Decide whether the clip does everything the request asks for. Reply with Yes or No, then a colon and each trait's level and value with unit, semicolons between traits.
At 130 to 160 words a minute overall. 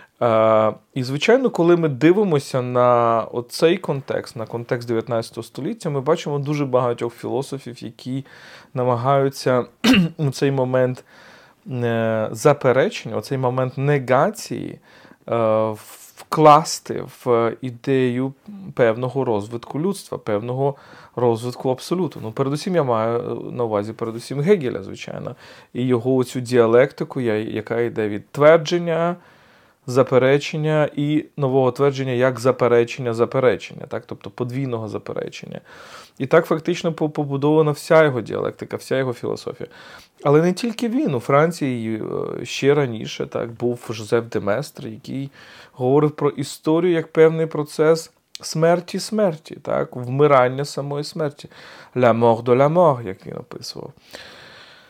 No: average, 120 wpm